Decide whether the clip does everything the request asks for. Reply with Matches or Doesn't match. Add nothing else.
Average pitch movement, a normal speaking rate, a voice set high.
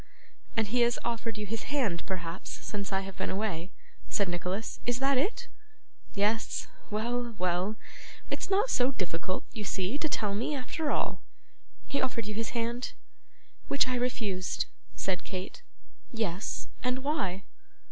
Matches